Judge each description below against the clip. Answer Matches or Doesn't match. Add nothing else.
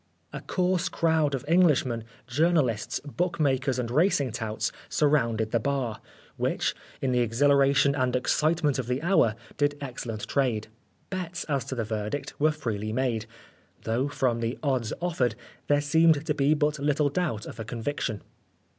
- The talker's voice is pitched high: Doesn't match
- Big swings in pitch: Doesn't match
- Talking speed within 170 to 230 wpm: Doesn't match